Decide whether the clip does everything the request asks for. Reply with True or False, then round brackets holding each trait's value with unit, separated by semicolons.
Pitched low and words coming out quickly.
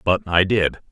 False (105 Hz; 195 wpm)